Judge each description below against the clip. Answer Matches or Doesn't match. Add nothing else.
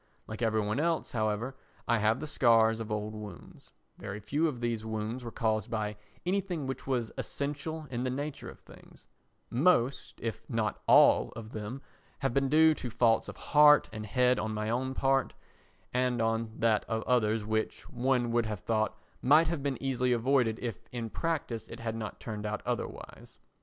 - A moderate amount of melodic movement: Matches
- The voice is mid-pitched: Doesn't match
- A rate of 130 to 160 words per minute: Doesn't match